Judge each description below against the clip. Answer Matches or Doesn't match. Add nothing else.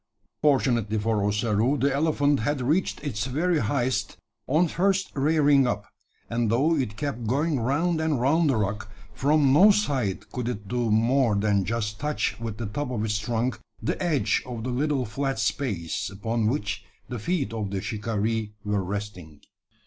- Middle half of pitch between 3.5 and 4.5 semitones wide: Doesn't match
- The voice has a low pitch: Matches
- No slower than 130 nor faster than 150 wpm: Doesn't match